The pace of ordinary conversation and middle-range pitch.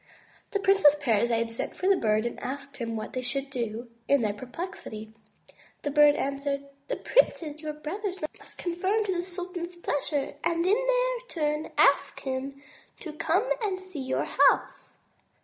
No: average, 165 wpm; very high, 300 Hz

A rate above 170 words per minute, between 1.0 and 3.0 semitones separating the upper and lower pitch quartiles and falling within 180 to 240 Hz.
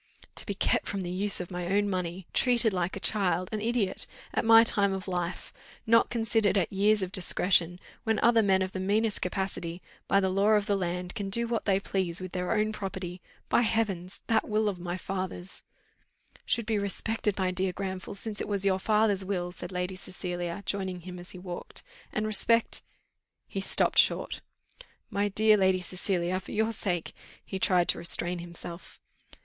Yes: average, 195 wpm; average, 2.7 semitones; high, 190 Hz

